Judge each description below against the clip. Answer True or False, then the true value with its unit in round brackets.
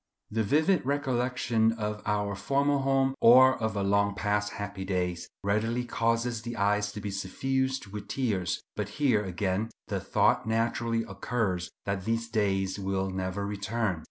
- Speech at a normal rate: True (150 wpm)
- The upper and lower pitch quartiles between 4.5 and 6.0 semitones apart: False (3.2 semitones)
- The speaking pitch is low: True (105 Hz)